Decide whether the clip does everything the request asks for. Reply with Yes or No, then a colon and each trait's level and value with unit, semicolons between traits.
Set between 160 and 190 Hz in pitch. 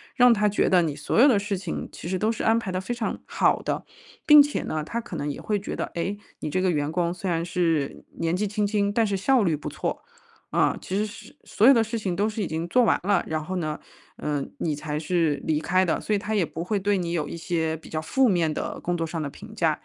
Yes: medium, 185 Hz